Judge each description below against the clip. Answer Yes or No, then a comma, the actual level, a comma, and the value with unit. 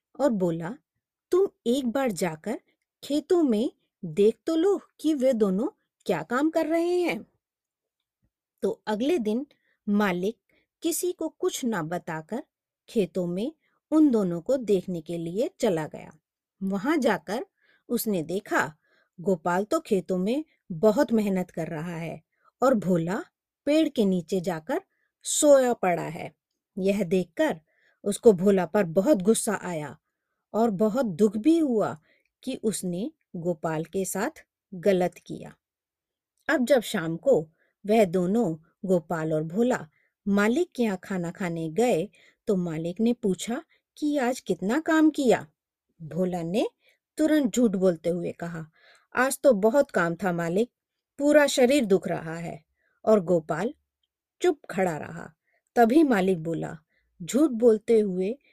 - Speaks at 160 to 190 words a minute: No, average, 135 wpm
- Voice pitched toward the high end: Yes, high, 215 Hz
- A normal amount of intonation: No, wide, 7.1 semitones